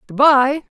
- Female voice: Yes, female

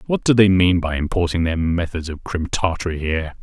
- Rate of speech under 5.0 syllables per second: No, 5.6 syllables/s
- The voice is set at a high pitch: No, very low, 85 Hz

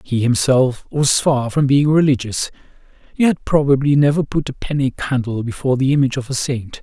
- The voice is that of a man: Yes, male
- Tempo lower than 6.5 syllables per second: Yes, 5.5 syllables/s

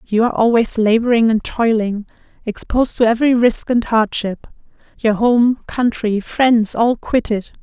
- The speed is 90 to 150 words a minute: Yes, average, 140 wpm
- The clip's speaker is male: No, female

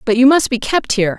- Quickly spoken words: Yes, fast, 305 wpm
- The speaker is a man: No, female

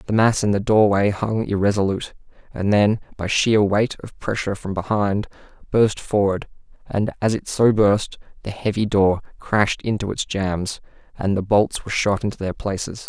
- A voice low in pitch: Yes, low, 100 Hz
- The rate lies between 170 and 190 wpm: Yes, average, 175 wpm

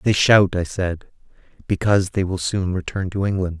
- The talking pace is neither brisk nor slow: Yes, average, 185 wpm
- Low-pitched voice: Yes, very low, 95 Hz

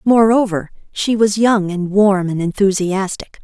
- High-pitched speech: Yes, high, 200 Hz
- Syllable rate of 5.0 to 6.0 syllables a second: No, 4.1 syllables/s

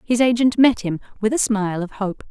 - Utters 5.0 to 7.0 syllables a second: Yes, 5.5 syllables/s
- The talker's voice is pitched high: Yes, high, 220 Hz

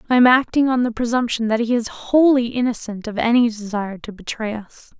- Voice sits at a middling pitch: No, high, 235 Hz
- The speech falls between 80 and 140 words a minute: No, fast, 205 wpm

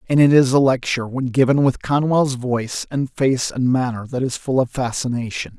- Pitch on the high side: No, low, 130 Hz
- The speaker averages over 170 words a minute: Yes, fast, 205 wpm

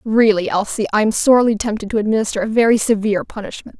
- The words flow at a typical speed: Yes, average, 190 wpm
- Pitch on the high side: Yes, high, 215 Hz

